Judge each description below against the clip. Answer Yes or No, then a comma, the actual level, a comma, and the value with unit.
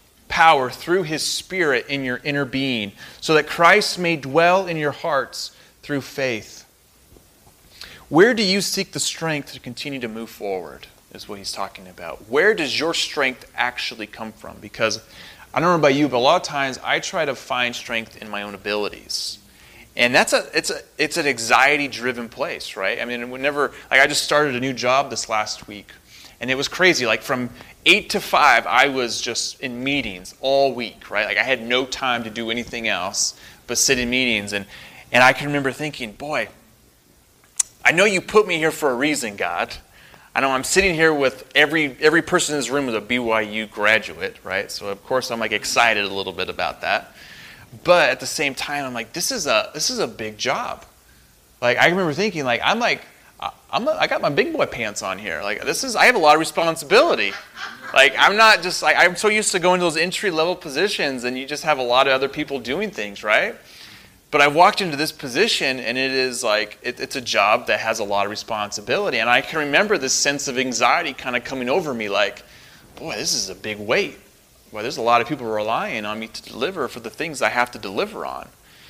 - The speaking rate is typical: No, fast, 215 wpm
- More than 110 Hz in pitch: Yes, low, 135 Hz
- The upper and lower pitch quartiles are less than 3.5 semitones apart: No, average, 4.9 semitones